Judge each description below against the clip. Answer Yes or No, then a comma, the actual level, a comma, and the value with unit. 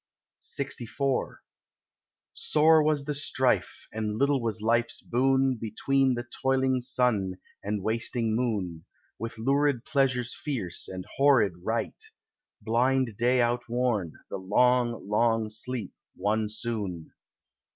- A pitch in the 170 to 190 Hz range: No, low, 120 Hz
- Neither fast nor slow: No, slow, 110 wpm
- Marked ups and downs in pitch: No, average, 3.5 semitones